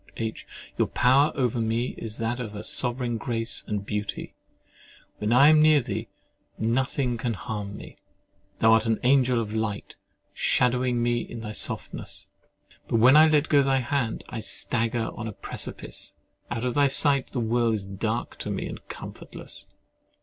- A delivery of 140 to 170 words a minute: Yes, average, 165 wpm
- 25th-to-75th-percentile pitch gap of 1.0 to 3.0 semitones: Yes, narrow, 2.5 semitones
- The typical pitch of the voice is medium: No, low, 120 Hz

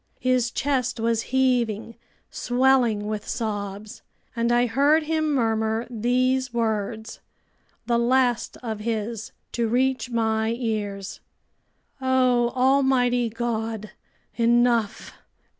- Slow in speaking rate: Yes, slow, 100 wpm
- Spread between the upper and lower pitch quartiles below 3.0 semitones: Yes, narrow, 2.4 semitones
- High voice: Yes, high, 235 Hz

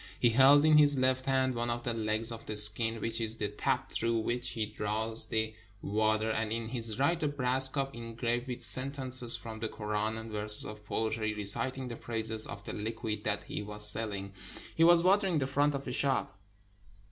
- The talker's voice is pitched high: No, low, 115 Hz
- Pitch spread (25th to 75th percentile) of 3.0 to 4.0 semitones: Yes, average, 3.3 semitones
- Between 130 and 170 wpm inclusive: No, fast, 205 wpm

